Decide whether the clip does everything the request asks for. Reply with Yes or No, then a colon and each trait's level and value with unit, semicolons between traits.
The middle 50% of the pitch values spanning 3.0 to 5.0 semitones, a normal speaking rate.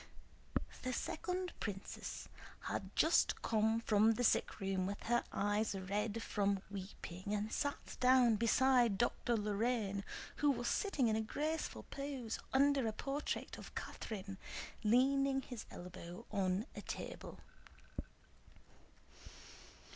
No: average, 4.2 semitones; slow, 115 wpm